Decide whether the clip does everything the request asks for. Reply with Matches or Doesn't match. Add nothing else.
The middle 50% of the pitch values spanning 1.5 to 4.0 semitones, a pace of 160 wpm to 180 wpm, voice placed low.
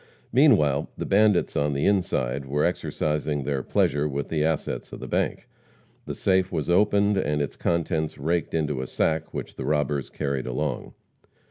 Matches